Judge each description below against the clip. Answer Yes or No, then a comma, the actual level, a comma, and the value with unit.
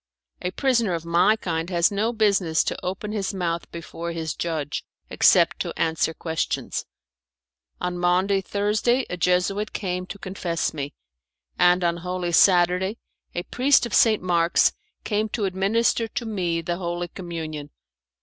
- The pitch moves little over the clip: No, average, 3.2 semitones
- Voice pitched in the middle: Yes, medium, 180 Hz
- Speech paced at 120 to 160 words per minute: Yes, average, 150 wpm